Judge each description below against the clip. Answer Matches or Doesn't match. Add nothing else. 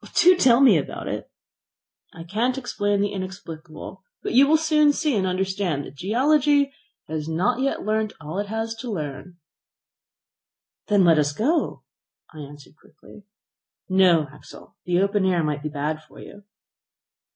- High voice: Matches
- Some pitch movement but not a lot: Doesn't match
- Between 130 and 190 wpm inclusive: Matches